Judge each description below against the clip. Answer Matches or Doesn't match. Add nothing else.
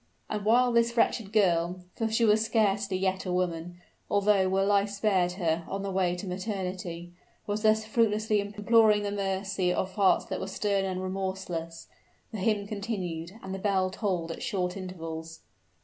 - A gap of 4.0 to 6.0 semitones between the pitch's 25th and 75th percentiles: Doesn't match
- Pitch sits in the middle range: Doesn't match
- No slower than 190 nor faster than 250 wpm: Doesn't match